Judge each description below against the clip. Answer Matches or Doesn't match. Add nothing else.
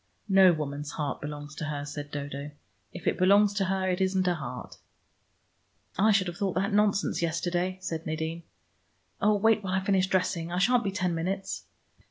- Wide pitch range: Doesn't match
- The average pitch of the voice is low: Doesn't match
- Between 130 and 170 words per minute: Doesn't match